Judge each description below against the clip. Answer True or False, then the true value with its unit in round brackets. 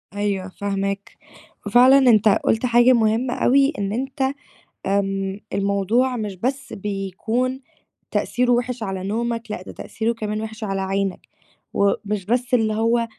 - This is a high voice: True (220 Hz)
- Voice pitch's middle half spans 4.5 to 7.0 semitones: False (3.6 semitones)